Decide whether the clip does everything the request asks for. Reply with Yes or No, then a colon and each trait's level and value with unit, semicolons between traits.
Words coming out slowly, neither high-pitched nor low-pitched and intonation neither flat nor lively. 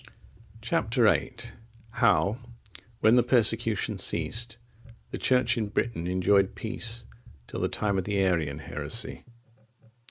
No: slow, 120 wpm; low, 110 Hz; average, 3.7 semitones